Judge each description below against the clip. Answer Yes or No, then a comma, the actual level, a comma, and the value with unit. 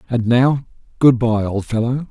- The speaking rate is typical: Yes, average, 170 wpm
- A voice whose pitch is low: Yes, low, 120 Hz